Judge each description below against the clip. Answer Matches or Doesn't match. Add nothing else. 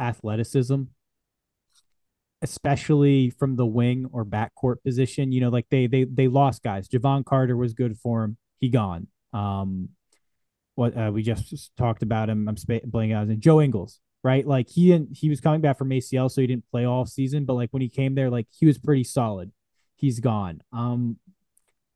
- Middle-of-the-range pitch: Doesn't match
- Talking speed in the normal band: Matches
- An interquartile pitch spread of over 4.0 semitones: Doesn't match